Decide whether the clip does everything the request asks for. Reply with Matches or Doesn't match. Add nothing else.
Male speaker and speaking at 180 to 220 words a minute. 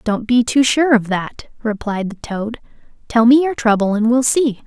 Doesn't match